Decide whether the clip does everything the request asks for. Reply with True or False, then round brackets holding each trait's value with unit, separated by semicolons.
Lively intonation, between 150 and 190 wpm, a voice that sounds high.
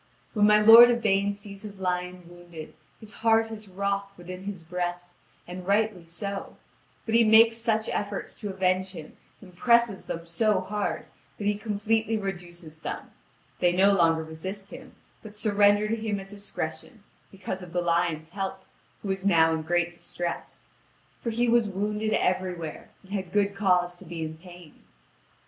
False (3.1 semitones; 165 wpm; 195 Hz)